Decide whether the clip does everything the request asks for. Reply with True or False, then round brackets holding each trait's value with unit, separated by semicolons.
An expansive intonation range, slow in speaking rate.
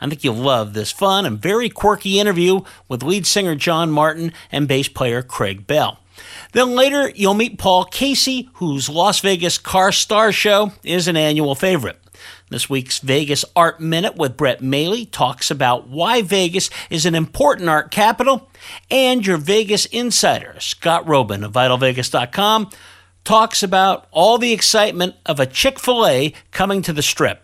False (6.7 semitones; 165 wpm)